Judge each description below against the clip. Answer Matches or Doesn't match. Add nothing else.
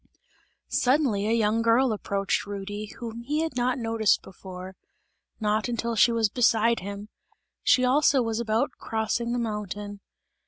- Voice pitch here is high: Matches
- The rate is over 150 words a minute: Doesn't match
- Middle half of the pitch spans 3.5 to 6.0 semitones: Doesn't match